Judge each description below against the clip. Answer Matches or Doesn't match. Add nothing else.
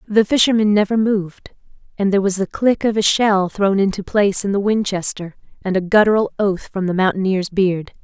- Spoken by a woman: Matches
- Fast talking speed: Doesn't match